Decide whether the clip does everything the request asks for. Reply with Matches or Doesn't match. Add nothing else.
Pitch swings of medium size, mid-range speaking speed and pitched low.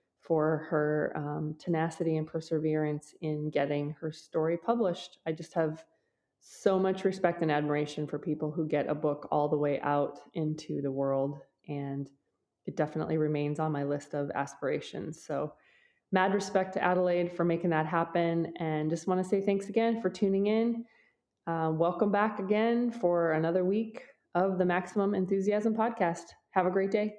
Doesn't match